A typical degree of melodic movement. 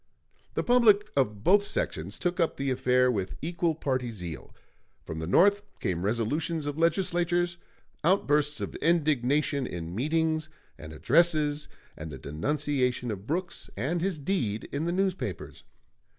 No: wide, 6.9 semitones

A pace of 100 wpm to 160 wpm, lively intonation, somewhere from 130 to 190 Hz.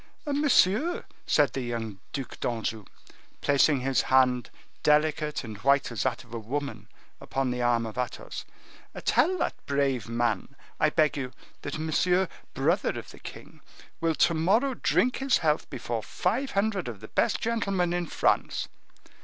Yes: average, 155 wpm; wide, 6.7 semitones; medium, 140 Hz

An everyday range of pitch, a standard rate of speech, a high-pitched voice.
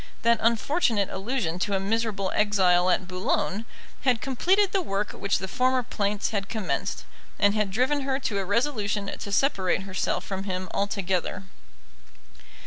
Yes: average, 3.5 semitones; average, 150 wpm; high, 205 Hz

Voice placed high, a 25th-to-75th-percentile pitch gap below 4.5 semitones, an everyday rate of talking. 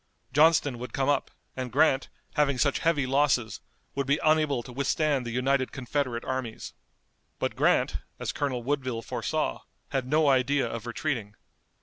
No: low, 135 Hz; narrow, 2.6 semitones; average, 150 wpm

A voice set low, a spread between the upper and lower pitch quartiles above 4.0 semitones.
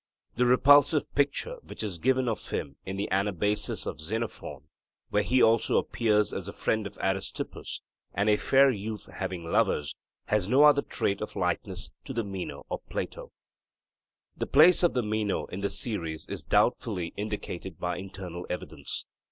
Yes: low, 105 Hz; average, 4.6 semitones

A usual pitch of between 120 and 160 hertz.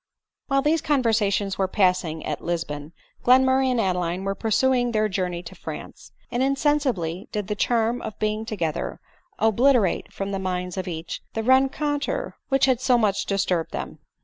No: high, 215 Hz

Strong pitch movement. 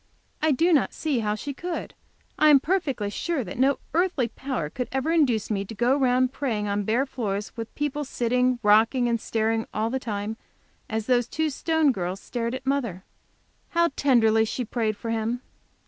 No: average, 4.1 semitones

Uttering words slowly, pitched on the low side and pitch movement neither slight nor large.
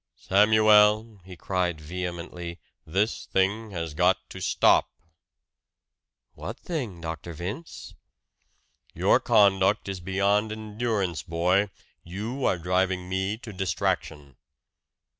Yes: slow, 105 wpm; very low, 95 Hz; average, 3.2 semitones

